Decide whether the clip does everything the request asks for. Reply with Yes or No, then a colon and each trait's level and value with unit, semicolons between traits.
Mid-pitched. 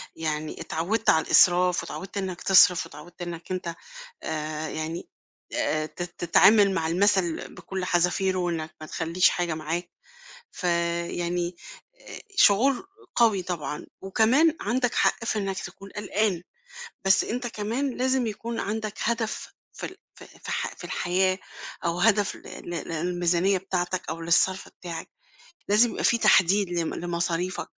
Yes: medium, 180 Hz